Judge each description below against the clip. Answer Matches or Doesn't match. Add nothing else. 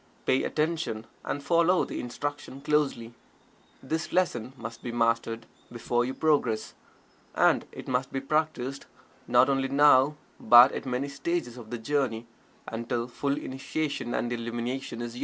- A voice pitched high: Doesn't match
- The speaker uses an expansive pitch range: Doesn't match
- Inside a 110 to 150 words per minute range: Matches